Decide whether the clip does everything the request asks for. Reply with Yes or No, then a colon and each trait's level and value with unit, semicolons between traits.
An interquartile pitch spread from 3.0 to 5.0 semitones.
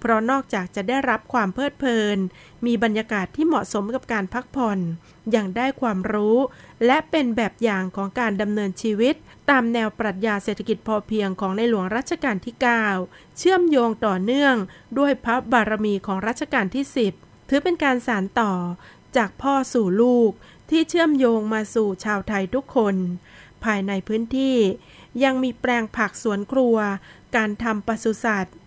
Yes: average, 3.4 semitones